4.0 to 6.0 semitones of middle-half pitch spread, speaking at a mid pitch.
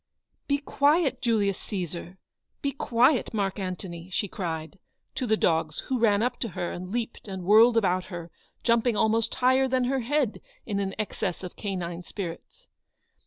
No: average, 5.2 semitones; high, 210 Hz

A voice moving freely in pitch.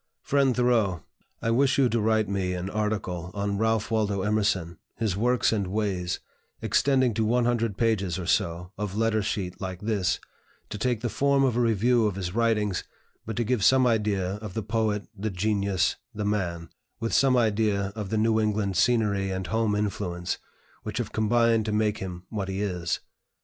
No: average, 2.8 semitones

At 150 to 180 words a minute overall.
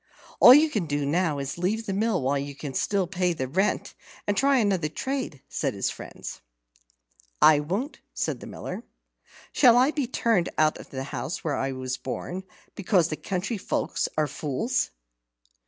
Yes: average, 175 wpm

